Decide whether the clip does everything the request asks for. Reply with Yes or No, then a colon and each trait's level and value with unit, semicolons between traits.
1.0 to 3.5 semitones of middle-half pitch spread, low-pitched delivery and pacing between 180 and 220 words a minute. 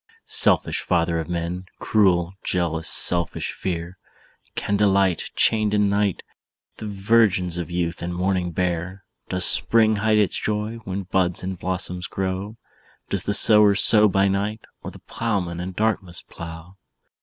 No: average, 2.8 semitones; very low, 95 Hz; average, 145 wpm